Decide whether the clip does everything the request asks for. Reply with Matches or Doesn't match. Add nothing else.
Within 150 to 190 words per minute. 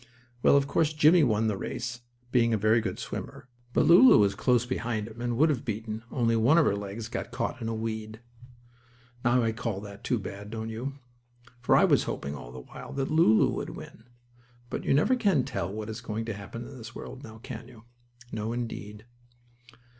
Doesn't match